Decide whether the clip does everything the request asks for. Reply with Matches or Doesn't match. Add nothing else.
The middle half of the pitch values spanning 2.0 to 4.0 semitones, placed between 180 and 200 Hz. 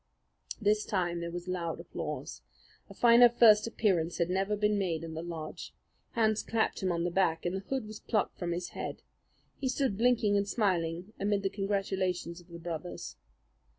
Matches